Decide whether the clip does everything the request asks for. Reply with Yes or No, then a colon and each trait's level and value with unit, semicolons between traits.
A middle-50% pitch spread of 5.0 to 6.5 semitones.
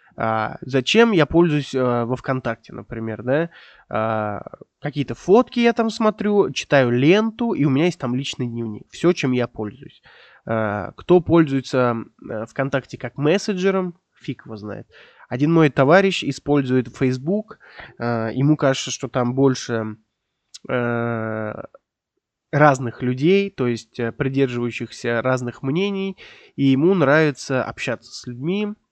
Yes: wide, 5.5 semitones